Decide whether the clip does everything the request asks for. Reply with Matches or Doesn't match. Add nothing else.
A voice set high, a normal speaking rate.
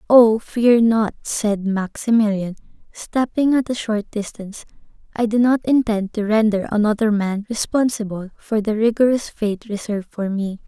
Matches